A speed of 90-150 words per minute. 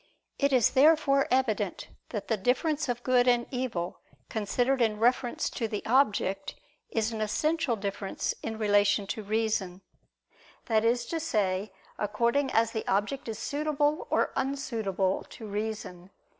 Yes: average, 145 wpm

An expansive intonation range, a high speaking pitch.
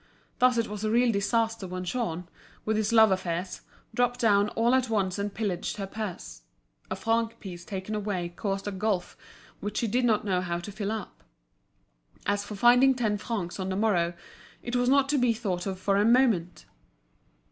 No: average, 3.5 semitones; high, 210 Hz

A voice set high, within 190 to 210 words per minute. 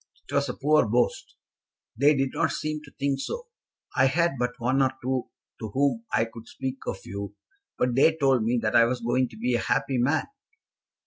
No: low, 130 Hz; fast, 205 wpm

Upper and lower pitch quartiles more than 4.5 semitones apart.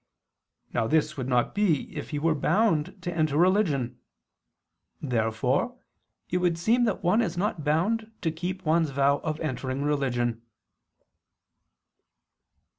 Yes: average, 4.9 semitones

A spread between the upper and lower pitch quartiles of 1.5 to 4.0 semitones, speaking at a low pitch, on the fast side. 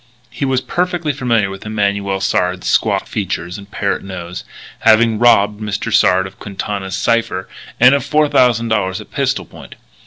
No: average, 3.5 semitones; low, 105 Hz; average, 150 wpm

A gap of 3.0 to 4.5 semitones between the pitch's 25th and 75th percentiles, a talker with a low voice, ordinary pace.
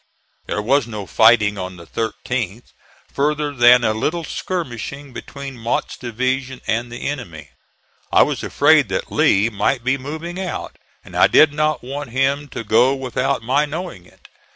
Yes: average, 4.2 semitones; low, 130 Hz; average, 160 wpm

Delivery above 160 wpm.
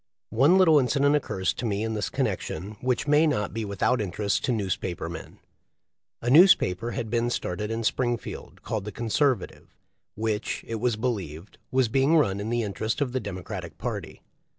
Yes: average, 175 wpm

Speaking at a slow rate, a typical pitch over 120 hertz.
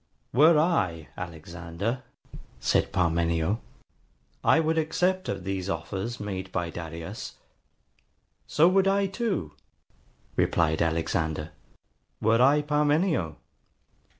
No: slow, 100 wpm; very low, 95 Hz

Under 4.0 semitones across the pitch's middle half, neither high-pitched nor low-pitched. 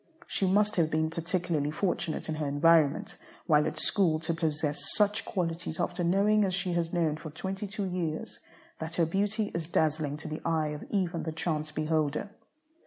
Yes: average, 3.0 semitones; medium, 165 Hz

